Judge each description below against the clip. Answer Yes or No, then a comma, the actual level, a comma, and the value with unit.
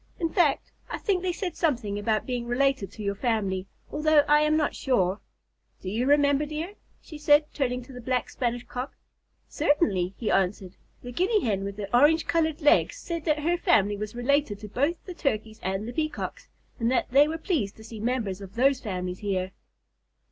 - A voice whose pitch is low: No, very high, 250 Hz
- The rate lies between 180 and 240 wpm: Yes, average, 195 wpm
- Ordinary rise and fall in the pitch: No, wide, 6.6 semitones